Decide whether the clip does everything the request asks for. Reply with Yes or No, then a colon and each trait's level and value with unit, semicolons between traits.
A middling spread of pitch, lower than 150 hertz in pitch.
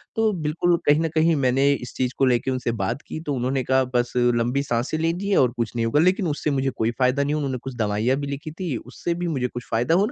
Yes: average, 4.4 semitones; low, 135 Hz